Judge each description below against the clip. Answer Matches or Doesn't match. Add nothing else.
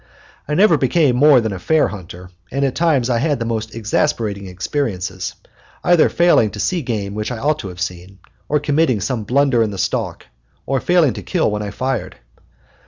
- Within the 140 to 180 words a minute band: Doesn't match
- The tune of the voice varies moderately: Doesn't match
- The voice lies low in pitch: Matches